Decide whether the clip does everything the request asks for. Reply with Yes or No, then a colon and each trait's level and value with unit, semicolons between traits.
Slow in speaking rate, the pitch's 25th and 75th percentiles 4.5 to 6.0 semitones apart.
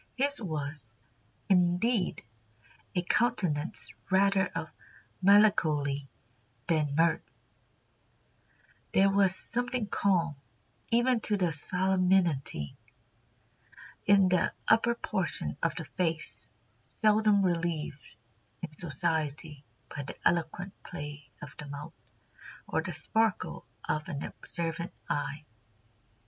Yes: slow, 95 wpm; average, 4.9 semitones